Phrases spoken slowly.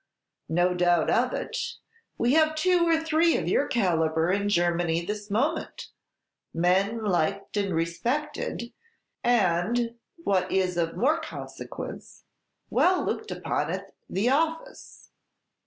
Yes: slow, 125 wpm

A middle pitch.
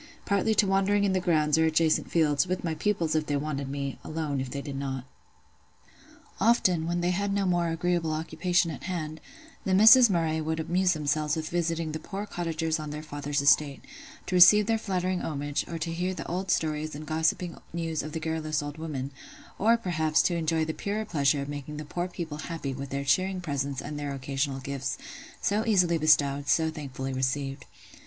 Yes: medium, 160 Hz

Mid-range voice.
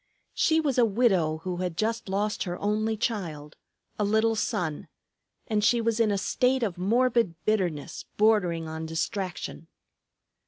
No: high, 210 Hz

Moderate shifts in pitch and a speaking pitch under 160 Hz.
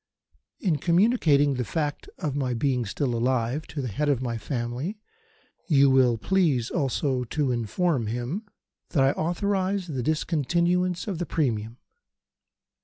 No: wide, 5.7 semitones; medium, 140 Hz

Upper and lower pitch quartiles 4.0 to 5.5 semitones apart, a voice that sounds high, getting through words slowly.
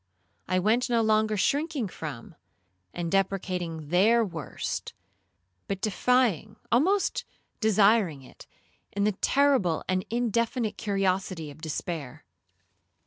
Yes: average, 4.8 semitones; high, 200 Hz; slow, 105 wpm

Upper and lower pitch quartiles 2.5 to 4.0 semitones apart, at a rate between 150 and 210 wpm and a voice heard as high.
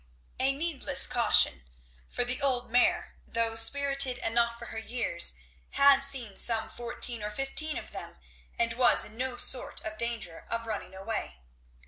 Yes: average, 2.9 semitones; average, 155 wpm; high, 235 Hz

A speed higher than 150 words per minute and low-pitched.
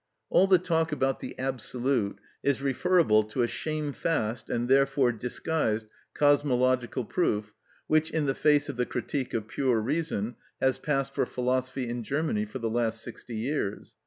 Yes: average, 160 wpm; low, 130 Hz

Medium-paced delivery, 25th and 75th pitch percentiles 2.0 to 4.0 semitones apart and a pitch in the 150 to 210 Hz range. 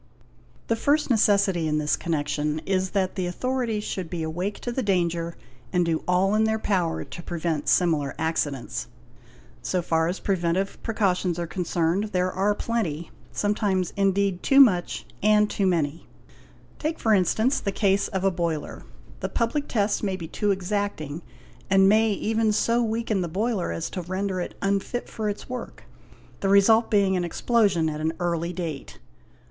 Yes: average, 165 wpm; average, 3.7 semitones; high, 190 Hz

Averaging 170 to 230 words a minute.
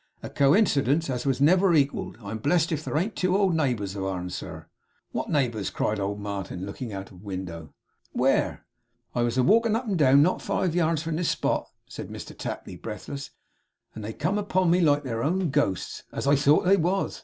Yes: average, 200 wpm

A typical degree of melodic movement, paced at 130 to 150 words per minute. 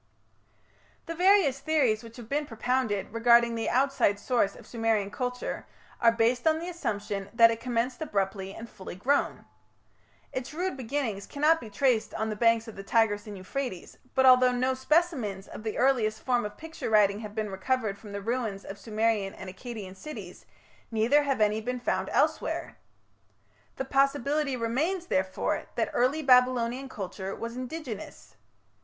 No: average, 4.0 semitones; average, 160 wpm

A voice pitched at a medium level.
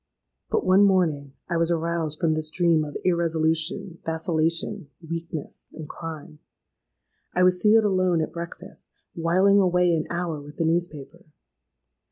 Yes: medium, 170 Hz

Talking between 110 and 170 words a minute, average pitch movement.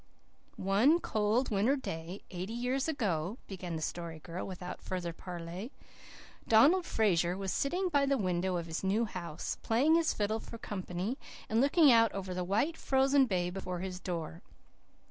No: average, 165 wpm; wide, 6.1 semitones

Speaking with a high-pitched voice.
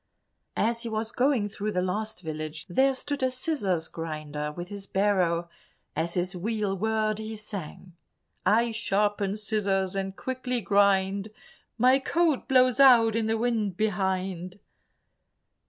Yes: high, 205 Hz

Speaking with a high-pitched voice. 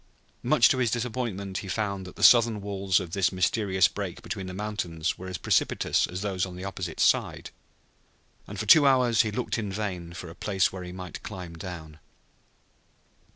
No: very low, 95 Hz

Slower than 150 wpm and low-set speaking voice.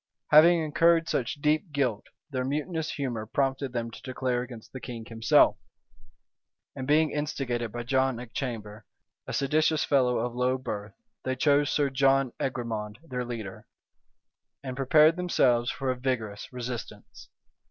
Yes: average, 140 wpm; low, 130 Hz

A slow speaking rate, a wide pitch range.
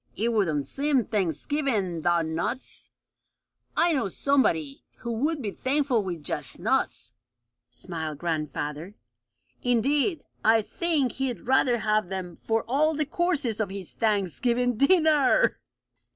Yes: slow, 125 wpm; wide, 7.6 semitones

